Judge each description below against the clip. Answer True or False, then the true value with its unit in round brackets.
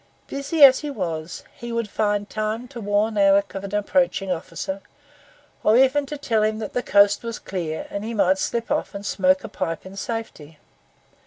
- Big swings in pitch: False (3.2 semitones)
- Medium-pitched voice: False (210 Hz)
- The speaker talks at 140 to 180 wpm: False (190 wpm)